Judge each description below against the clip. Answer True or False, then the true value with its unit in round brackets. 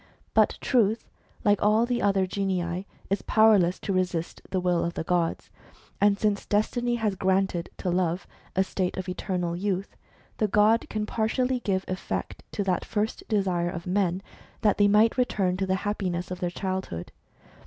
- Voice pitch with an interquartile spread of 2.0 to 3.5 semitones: True (2.6 semitones)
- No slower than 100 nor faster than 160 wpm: False (170 wpm)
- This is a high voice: True (195 Hz)